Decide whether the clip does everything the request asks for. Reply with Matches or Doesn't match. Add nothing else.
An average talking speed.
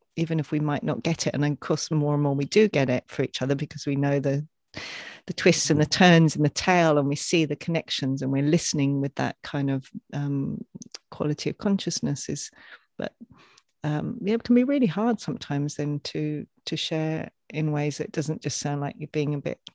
Doesn't match